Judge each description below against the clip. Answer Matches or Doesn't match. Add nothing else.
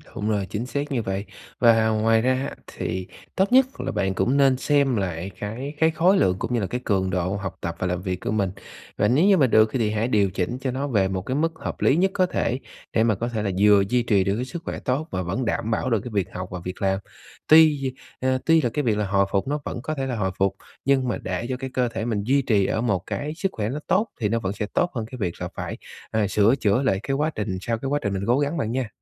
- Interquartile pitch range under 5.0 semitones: Doesn't match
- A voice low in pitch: Matches